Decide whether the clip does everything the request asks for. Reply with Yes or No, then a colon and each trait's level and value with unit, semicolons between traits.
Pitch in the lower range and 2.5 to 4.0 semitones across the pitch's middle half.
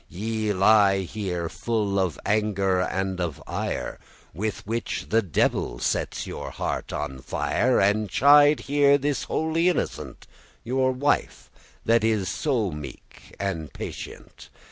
No: low, 105 Hz; average, 5.2 semitones